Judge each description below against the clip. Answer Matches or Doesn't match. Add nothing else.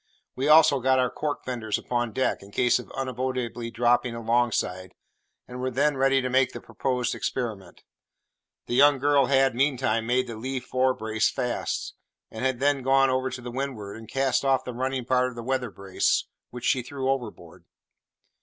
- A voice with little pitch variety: Matches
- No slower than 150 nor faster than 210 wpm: Matches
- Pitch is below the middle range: Matches